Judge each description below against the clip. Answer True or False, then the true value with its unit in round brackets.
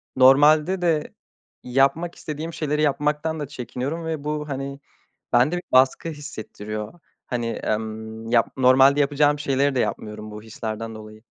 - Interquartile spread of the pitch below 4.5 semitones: False (4.8 semitones)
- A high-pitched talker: False (135 Hz)